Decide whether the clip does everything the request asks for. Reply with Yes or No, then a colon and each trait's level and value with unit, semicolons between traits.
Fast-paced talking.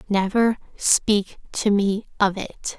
No: slow, 130 wpm